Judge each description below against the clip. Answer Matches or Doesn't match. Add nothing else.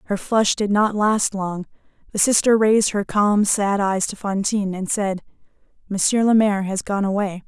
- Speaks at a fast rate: Doesn't match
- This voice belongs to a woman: Matches